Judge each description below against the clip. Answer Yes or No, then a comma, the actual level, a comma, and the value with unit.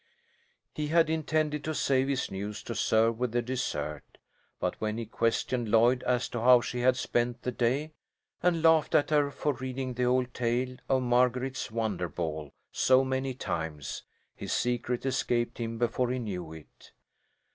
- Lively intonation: No, narrow, 2.5 semitones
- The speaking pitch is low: Yes, low, 125 Hz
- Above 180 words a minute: No, average, 170 wpm